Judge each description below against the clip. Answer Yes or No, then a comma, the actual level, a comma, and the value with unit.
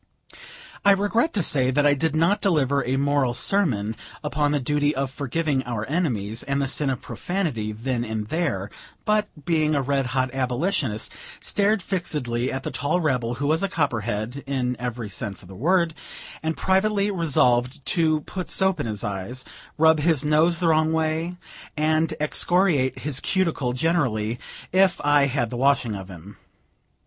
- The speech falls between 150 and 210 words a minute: Yes, average, 170 wpm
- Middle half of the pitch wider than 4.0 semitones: Yes, average, 5.1 semitones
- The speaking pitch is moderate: Yes, medium, 145 Hz